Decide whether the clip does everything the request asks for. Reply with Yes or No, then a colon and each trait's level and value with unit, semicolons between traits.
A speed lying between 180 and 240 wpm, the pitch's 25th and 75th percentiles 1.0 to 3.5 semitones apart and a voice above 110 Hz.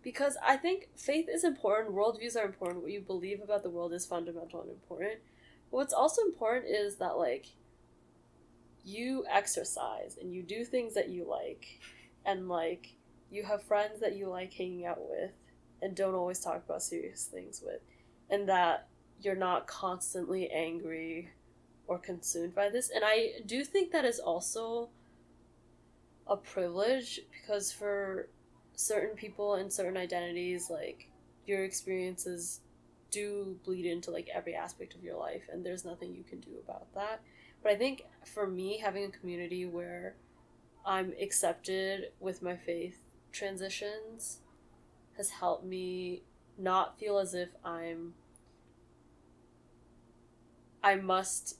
No: average, 145 wpm; average, 2.9 semitones; high, 190 Hz